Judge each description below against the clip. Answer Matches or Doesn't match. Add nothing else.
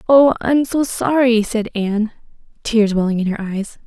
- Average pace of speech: Matches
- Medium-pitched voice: Doesn't match